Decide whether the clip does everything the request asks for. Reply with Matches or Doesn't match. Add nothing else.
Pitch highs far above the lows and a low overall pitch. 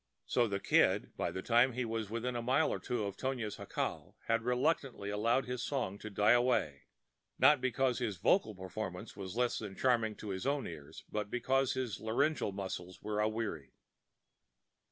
Doesn't match